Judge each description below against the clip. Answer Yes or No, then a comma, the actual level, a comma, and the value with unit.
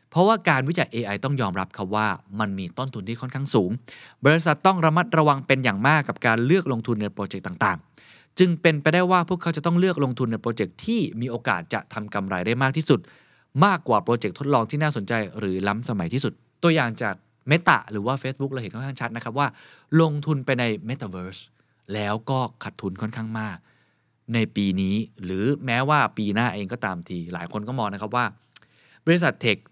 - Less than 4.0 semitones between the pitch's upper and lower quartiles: No, wide, 5.4 semitones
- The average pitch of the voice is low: Yes, low, 120 Hz